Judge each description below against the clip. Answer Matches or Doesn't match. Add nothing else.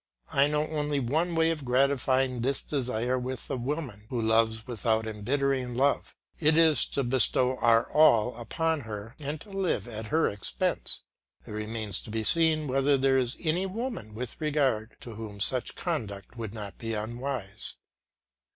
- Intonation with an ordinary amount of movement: Matches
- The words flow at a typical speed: Matches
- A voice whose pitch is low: Matches